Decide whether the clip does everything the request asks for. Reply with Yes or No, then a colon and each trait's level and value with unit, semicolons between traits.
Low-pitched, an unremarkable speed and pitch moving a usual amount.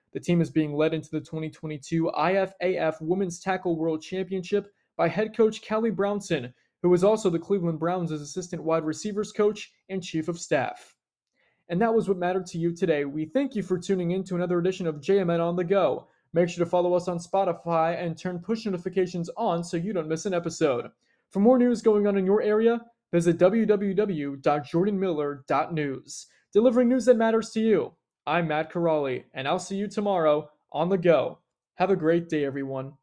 No: medium, 180 Hz; average, 190 wpm; average, 3.6 semitones